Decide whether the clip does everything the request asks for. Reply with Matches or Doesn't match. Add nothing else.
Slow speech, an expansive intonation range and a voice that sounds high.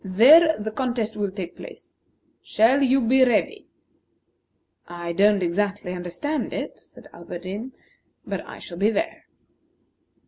Matches